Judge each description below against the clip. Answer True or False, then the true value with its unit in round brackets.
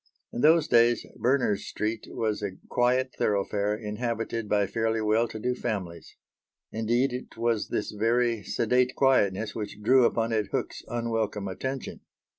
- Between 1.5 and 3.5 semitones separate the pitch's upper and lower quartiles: True (2.6 semitones)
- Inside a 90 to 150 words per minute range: True (145 wpm)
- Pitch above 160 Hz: False (115 Hz)